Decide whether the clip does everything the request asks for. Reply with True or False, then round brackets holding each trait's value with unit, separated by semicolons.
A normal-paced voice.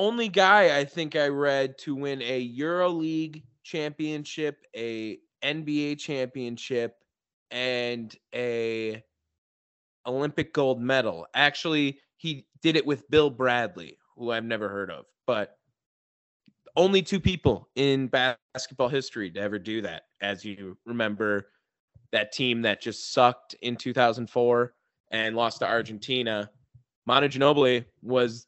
False (125 wpm)